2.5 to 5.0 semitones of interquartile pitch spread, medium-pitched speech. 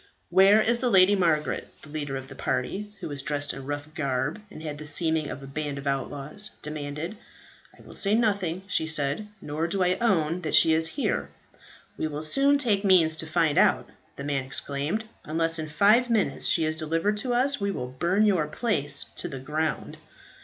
No: wide, 5.5 semitones; medium, 160 Hz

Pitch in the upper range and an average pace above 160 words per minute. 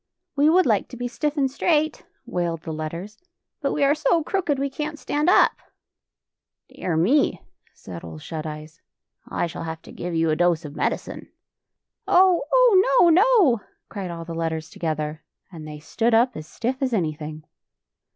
Yes: high, 200 Hz; average, 190 wpm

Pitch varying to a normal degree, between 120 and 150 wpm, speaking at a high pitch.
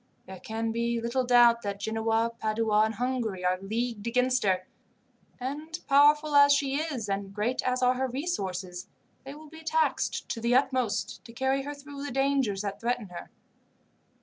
No: average, 4.2 semitones; average, 175 wpm; high, 240 Hz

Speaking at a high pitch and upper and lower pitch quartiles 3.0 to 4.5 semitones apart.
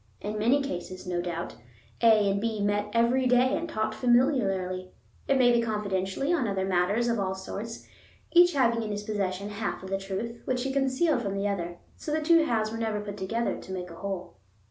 Yes: high, 215 Hz; average, 4.1 semitones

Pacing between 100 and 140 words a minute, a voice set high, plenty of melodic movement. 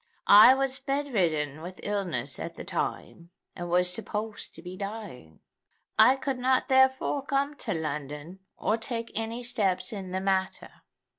No: average, 155 wpm; high, 205 Hz; wide, 6.0 semitones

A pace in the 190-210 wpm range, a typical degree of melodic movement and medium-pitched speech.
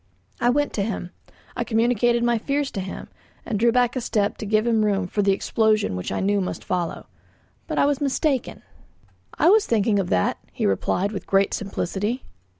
No: average, 195 wpm; average, 3.6 semitones; high, 215 Hz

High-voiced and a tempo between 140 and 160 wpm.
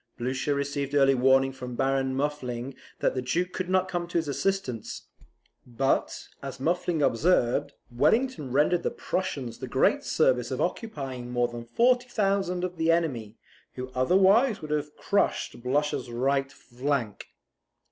No: medium, 140 Hz; average, 145 wpm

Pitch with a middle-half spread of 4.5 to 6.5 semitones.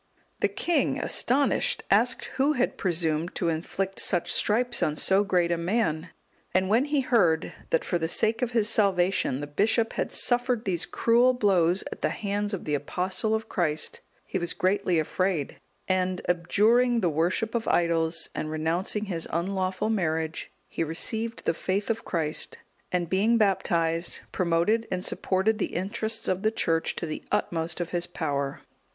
Yes: average, 4.8 semitones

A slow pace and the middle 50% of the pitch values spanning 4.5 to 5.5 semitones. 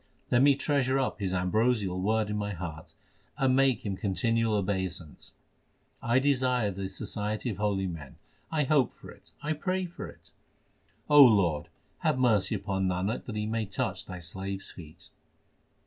No: average, 160 wpm; average, 5.2 semitones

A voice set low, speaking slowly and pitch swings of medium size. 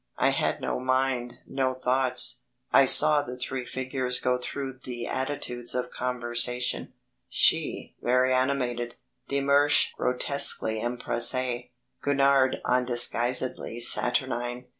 No: low, 125 Hz; slow, 110 wpm; narrow, 1.4 semitones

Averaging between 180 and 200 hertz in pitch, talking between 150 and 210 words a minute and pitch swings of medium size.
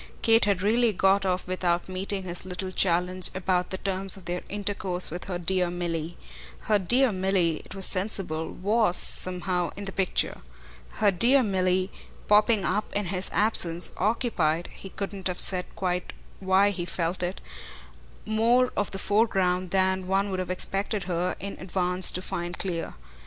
No: medium, 185 Hz; average, 165 wpm; narrow, 2.0 semitones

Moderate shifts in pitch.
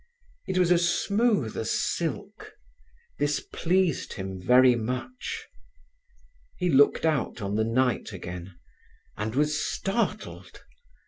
No: wide, 8.5 semitones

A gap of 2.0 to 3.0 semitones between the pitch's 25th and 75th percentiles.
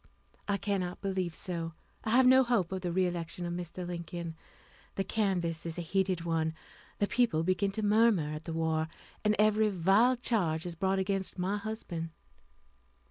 No: average, 3.5 semitones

